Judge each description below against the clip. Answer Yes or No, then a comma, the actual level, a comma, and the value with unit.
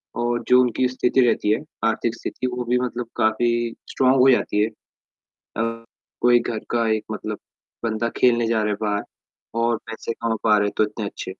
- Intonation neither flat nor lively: No, narrow, 1.9 semitones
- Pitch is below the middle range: Yes, low, 115 Hz